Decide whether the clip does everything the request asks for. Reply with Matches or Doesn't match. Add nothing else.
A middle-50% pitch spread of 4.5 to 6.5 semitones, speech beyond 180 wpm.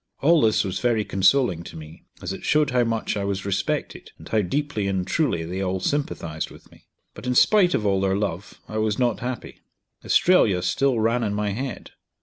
Matches